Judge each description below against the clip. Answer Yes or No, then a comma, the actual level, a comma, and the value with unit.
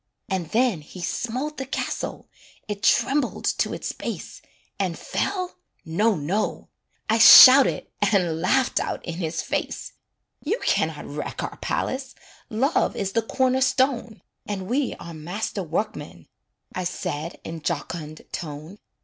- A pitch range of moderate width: No, wide, 7.3 semitones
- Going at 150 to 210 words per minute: No, average, 140 wpm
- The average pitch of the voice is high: Yes, high, 210 Hz